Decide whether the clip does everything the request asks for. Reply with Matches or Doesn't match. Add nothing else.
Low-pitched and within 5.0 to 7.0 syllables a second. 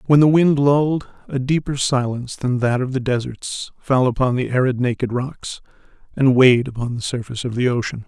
Matches